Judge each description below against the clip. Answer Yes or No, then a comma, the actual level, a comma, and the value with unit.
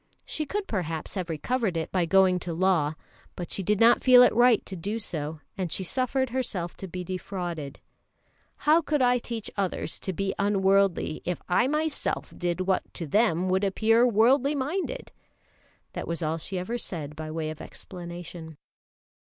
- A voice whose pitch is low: No, high, 190 Hz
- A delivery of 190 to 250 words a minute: No, average, 175 wpm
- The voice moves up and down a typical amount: No, wide, 5.7 semitones